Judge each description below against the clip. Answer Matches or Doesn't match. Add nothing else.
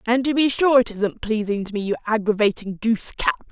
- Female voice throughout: Matches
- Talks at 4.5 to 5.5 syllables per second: Doesn't match